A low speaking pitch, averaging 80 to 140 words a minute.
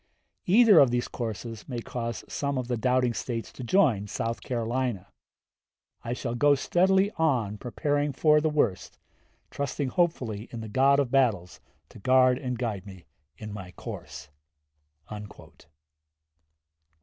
Yes: low, 125 Hz; slow, 135 wpm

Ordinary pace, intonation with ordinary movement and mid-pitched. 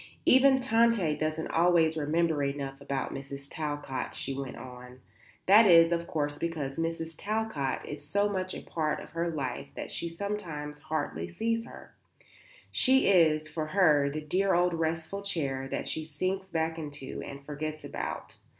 Yes: average, 160 wpm; average, 3.7 semitones; medium, 160 Hz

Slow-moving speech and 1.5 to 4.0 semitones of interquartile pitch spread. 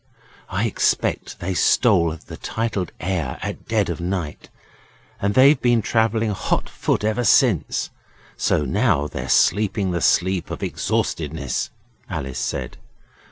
No: slow, 130 wpm; average, 5.3 semitones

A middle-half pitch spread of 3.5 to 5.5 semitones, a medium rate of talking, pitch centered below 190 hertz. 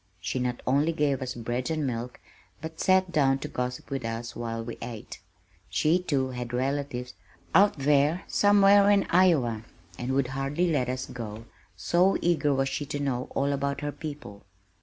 Yes: average, 4.1 semitones; average, 175 wpm; low, 135 Hz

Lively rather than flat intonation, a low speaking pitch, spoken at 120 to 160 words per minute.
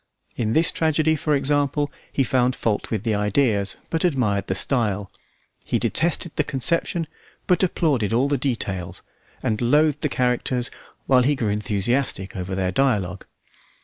Yes: wide, 5.9 semitones; low, 125 Hz; average, 150 wpm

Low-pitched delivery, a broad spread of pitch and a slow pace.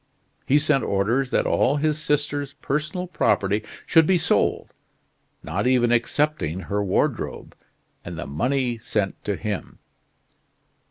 Yes: low, 130 Hz; wide, 6.4 semitones; slow, 125 wpm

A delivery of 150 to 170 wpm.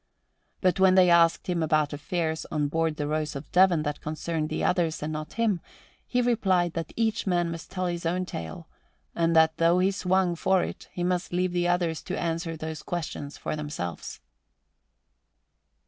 No: average, 180 wpm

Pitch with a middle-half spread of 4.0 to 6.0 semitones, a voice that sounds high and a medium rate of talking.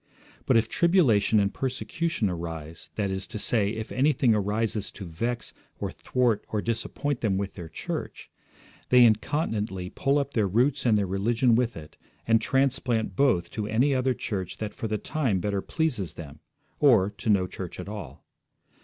No: average, 4.5 semitones; low, 110 Hz; average, 170 wpm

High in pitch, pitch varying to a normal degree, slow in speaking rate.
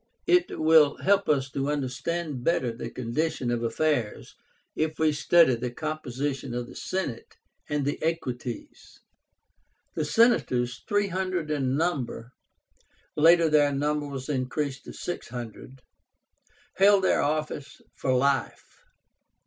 No: medium, 145 Hz; average, 4.1 semitones; slow, 125 wpm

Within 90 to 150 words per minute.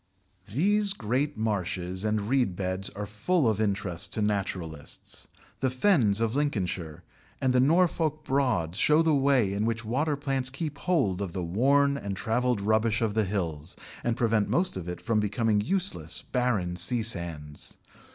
No: average, 160 wpm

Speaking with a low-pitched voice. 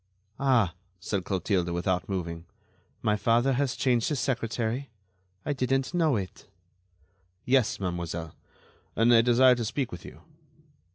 Yes: low, 115 Hz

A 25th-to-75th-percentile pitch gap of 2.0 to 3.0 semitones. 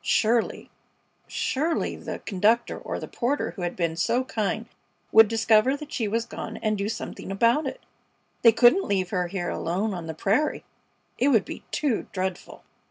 No: average, 4.0 semitones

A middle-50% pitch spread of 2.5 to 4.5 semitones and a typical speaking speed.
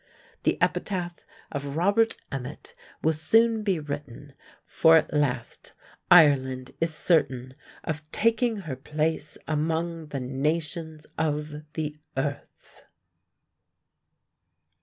No: average, 2.8 semitones; slow, 100 wpm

